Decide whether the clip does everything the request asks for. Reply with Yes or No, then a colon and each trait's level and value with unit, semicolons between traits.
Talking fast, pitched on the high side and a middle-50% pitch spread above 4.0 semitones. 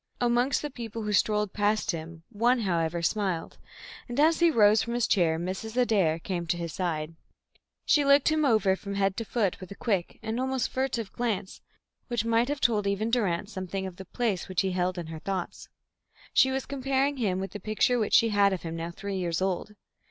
Yes: fast, 210 wpm; high, 205 Hz; average, 4.5 semitones